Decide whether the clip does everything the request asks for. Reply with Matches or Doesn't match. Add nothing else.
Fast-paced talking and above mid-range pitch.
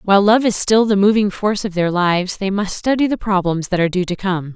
Matches